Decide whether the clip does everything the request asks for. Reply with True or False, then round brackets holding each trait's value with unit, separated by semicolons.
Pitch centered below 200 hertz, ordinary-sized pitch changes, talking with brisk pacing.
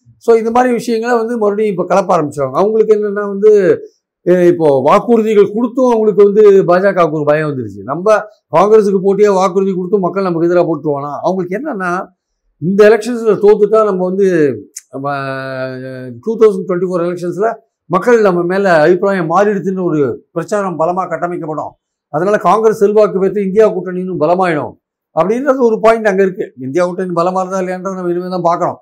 True (190 Hz; 3.6 semitones; 150 wpm)